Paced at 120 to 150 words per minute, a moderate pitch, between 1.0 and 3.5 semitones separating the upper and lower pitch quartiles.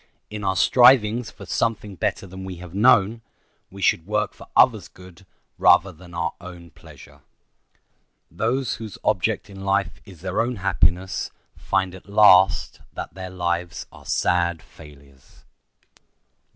No: average, 140 wpm; very low, 95 Hz; average, 3.1 semitones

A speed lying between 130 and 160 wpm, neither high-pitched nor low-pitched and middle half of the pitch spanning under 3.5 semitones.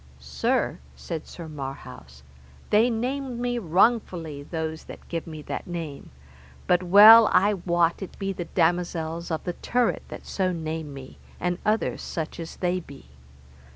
No: average, 155 wpm; medium, 175 Hz; average, 3.9 semitones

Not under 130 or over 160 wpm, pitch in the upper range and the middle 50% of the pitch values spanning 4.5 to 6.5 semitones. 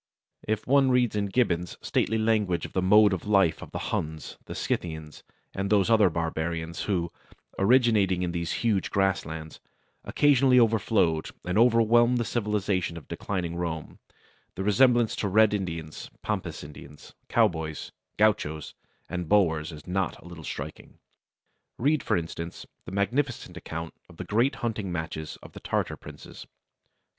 No: average, 150 wpm; very low, 95 Hz; average, 4.9 semitones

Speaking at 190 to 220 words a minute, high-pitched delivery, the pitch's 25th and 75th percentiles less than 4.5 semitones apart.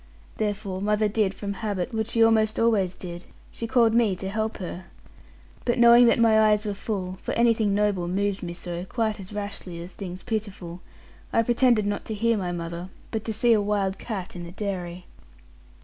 Yes: average, 195 wpm; high, 205 Hz; average, 3.1 semitones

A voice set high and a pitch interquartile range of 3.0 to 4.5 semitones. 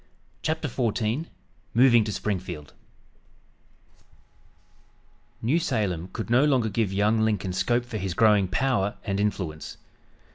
No: low, 110 Hz; average, 3.9 semitones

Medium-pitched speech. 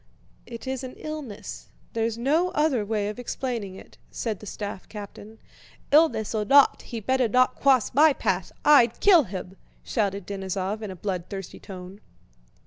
No: high, 225 Hz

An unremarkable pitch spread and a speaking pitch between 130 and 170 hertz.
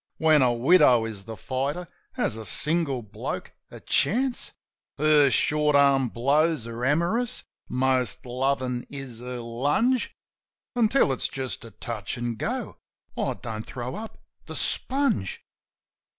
Yes: average, 4.5 semitones; low, 135 Hz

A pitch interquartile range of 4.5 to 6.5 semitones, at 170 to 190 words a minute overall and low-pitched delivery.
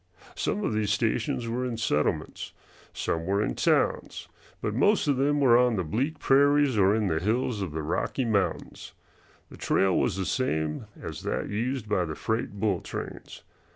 Yes: average, 4.9 semitones; average, 180 wpm; low, 110 Hz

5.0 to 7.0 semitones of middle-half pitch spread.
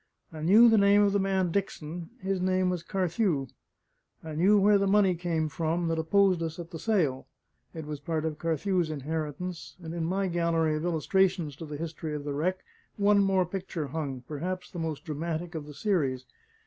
No: average, 3.4 semitones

